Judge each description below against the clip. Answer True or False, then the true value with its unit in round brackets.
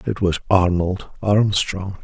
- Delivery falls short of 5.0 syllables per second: True (3.6 syllables/s)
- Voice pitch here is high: False (95 Hz)